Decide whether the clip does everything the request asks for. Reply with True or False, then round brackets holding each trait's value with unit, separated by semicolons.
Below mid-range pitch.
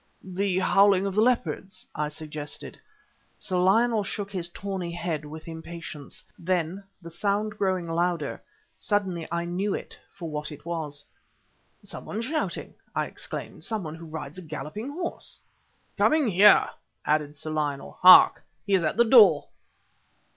False (180 Hz)